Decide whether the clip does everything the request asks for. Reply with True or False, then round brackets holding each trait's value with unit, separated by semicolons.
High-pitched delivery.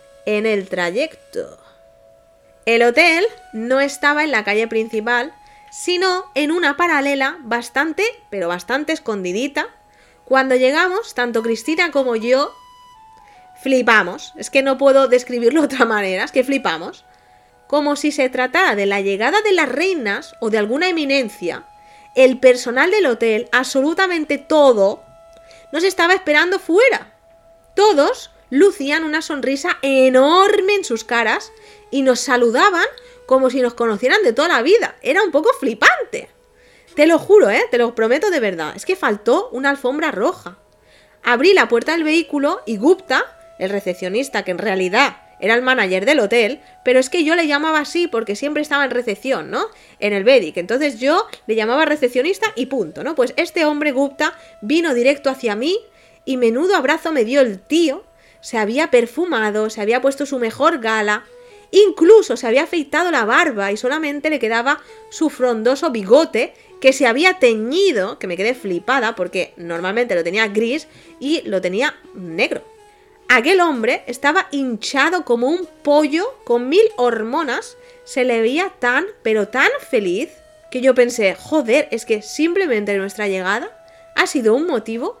True (275 Hz)